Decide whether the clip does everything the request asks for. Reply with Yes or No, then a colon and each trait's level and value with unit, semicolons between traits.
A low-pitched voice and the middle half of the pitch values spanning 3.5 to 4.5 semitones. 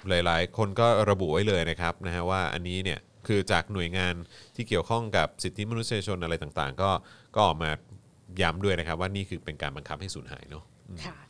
No: very low, 95 Hz; average, 3.0 semitones